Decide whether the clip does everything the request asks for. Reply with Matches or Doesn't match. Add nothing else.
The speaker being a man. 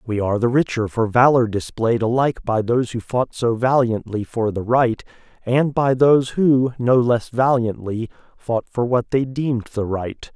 Matches